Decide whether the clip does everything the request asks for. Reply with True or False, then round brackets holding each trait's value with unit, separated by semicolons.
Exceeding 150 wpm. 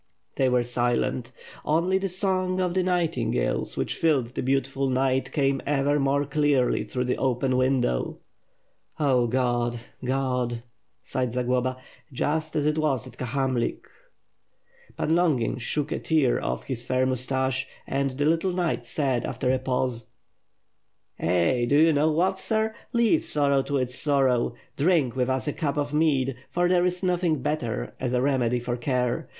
True (160 wpm)